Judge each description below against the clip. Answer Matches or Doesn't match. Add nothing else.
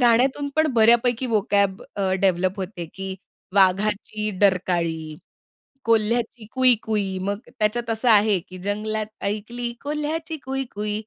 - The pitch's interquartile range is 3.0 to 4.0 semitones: Matches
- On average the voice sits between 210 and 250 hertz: Matches